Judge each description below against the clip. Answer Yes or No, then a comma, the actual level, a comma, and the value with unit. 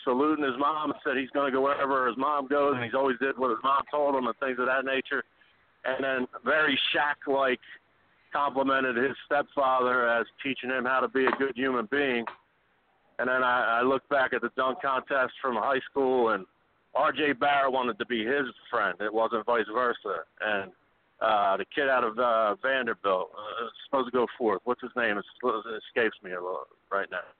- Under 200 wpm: No, fast, 205 wpm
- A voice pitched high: No, low, 135 Hz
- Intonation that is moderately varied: No, narrow, 1.8 semitones